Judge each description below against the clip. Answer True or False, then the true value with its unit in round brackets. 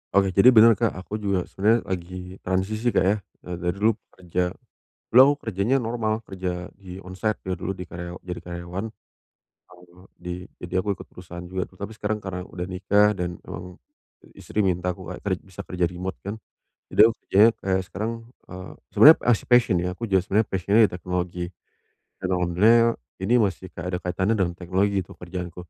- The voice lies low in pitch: True (95 Hz)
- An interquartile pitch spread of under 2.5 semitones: False (2.8 semitones)